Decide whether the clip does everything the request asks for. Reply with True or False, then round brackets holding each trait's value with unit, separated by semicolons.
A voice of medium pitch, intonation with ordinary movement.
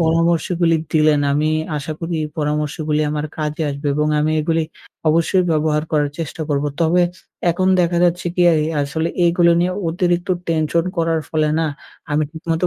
False (160 Hz; 1.8 semitones)